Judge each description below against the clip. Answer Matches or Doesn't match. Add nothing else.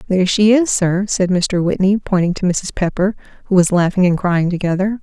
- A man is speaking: Doesn't match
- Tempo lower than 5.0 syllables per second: Doesn't match